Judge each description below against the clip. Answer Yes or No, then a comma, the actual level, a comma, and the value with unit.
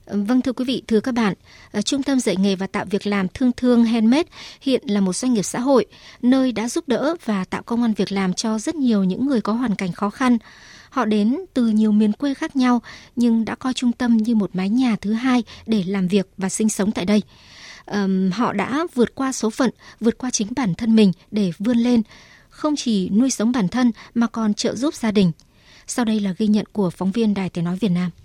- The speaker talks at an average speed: Yes, average, 240 wpm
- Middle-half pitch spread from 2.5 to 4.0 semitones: Yes, average, 3.6 semitones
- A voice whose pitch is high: Yes, high, 225 Hz